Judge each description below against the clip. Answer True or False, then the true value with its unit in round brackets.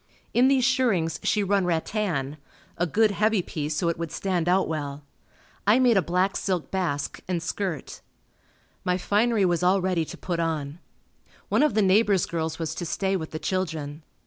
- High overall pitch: False (180 Hz)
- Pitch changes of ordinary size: True (3.9 semitones)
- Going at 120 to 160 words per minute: False (180 wpm)